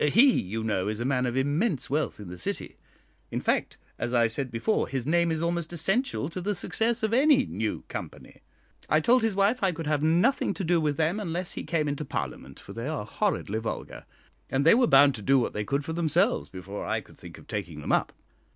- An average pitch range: No, wide, 7.5 semitones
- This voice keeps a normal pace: No, fast, 230 wpm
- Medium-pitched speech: Yes, medium, 155 Hz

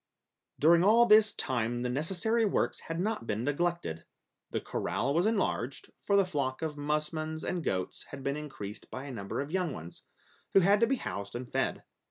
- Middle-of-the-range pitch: Yes, medium, 150 Hz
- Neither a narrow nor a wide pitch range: No, wide, 6.7 semitones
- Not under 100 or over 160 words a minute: No, average, 190 wpm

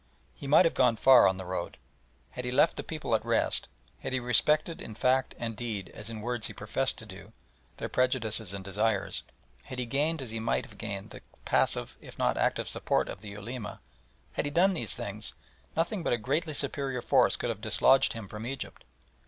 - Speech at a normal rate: No, fast, 210 wpm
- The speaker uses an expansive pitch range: No, average, 4.1 semitones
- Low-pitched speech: Yes, low, 120 Hz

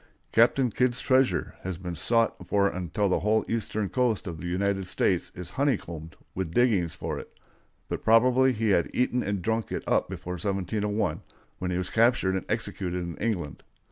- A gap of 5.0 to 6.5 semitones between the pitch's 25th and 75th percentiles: No, average, 4.2 semitones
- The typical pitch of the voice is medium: No, low, 100 Hz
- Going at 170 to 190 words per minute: Yes, average, 175 wpm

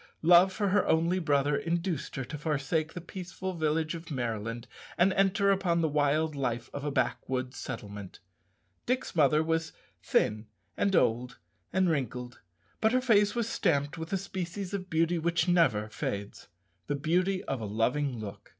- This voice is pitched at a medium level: Yes, medium, 160 Hz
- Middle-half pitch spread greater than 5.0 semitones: Yes, wide, 5.6 semitones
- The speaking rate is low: No, average, 165 wpm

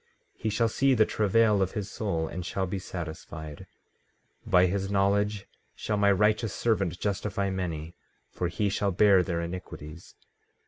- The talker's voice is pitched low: Yes, very low, 95 Hz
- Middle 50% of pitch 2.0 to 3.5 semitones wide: Yes, average, 3.0 semitones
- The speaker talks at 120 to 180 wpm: Yes, average, 155 wpm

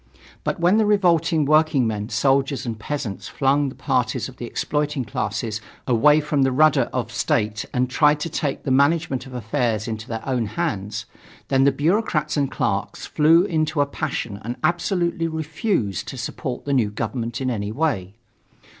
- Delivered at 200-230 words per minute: No, average, 170 wpm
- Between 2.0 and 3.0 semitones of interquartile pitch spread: No, average, 5.0 semitones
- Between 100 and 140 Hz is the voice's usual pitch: Yes, low, 135 Hz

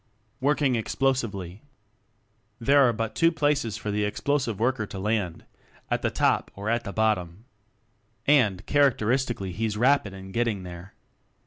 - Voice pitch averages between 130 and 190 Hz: No, low, 110 Hz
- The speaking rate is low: No, average, 145 wpm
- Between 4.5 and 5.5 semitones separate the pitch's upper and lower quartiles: Yes, average, 4.9 semitones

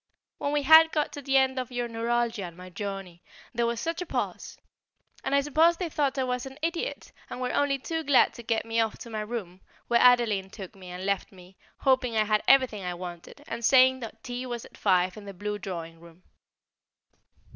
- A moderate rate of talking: No, fast, 215 wpm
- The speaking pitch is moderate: No, high, 235 Hz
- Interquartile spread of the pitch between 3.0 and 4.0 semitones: No, wide, 5.4 semitones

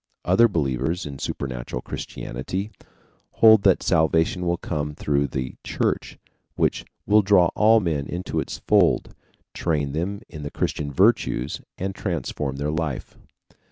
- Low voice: Yes, very low, 80 Hz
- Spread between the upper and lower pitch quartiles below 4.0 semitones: No, average, 5.0 semitones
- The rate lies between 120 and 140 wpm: Yes, slow, 135 wpm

